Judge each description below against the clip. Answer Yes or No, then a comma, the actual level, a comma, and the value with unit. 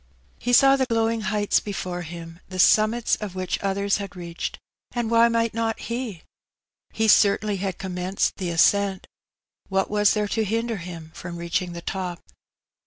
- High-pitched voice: Yes, high, 200 Hz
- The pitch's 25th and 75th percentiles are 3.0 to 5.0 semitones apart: Yes, average, 3.8 semitones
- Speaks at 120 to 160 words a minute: No, average, 170 wpm